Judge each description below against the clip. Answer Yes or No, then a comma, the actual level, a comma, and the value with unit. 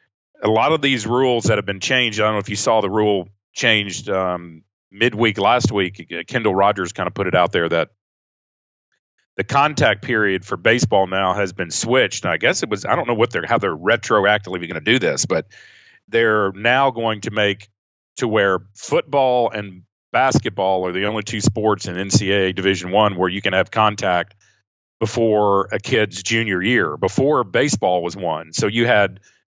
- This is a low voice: Yes, low, 105 Hz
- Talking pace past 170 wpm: Yes, average, 190 wpm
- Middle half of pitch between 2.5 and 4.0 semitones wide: Yes, average, 2.9 semitones